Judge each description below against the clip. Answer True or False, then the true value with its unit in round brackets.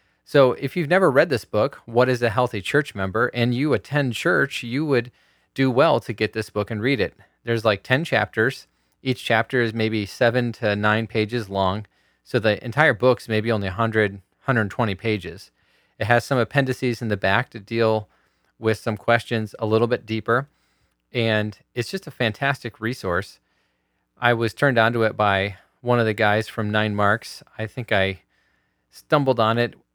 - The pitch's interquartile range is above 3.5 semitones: False (2.9 semitones)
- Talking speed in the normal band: True (180 wpm)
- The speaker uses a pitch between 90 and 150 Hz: True (115 Hz)